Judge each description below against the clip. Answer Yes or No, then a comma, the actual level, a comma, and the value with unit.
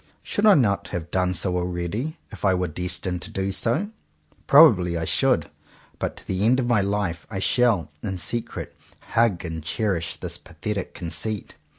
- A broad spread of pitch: No, average, 4.2 semitones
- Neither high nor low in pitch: No, very low, 95 Hz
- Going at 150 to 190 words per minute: Yes, average, 175 wpm